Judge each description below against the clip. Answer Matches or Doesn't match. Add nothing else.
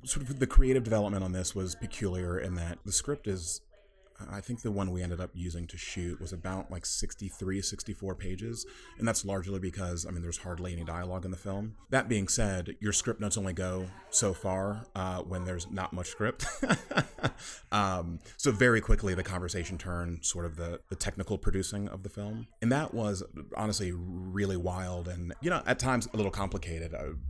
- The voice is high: Doesn't match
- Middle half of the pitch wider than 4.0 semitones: Doesn't match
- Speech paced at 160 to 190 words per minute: Doesn't match